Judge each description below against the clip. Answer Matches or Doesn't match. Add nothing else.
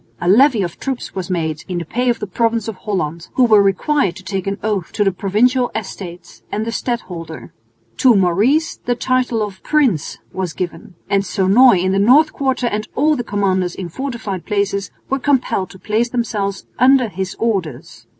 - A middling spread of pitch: Matches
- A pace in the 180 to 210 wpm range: Matches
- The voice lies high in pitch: Matches